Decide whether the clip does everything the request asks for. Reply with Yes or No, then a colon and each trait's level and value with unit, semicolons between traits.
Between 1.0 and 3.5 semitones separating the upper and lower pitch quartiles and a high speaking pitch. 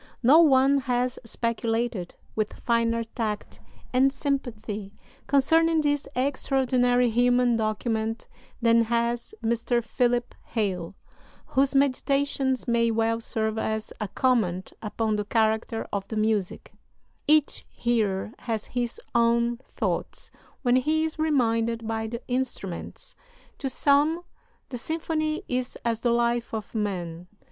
Yes: average, 2.9 semitones; high, 235 Hz